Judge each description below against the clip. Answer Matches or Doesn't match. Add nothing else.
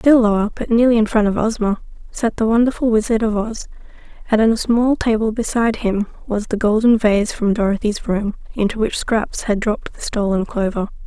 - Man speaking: Doesn't match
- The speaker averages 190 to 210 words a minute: Matches